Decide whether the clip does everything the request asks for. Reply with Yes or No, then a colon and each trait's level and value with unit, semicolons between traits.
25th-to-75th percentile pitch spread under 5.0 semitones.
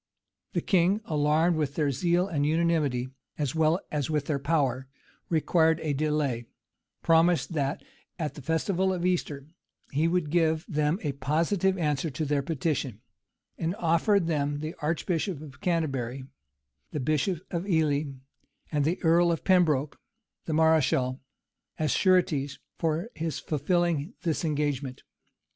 Yes: average, 2.9 semitones